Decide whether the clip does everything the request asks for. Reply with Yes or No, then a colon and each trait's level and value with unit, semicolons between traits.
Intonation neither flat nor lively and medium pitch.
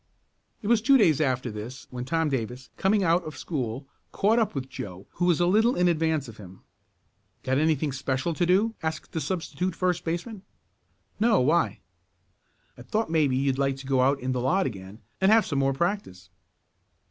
No: wide, 5.8 semitones; medium, 155 Hz